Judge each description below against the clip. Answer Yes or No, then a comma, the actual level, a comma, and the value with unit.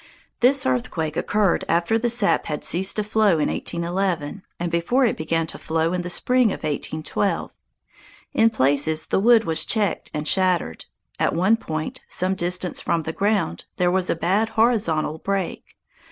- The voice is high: No, medium, 180 Hz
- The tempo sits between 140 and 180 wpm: Yes, average, 170 wpm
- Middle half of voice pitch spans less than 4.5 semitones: No, average, 4.8 semitones